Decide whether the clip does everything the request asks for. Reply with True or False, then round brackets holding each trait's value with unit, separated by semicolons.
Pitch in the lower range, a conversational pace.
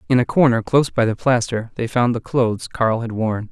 False (120 Hz; 240 wpm)